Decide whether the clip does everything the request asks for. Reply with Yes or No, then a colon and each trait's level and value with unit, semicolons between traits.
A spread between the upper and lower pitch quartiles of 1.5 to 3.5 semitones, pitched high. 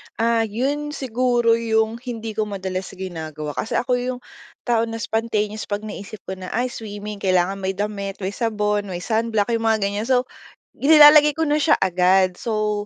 Yes: average, 3.2 semitones; high, 220 Hz